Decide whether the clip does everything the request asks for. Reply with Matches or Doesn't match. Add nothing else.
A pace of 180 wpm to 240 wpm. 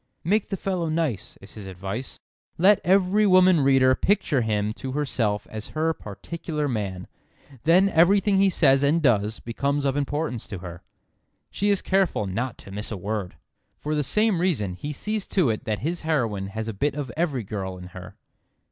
Matches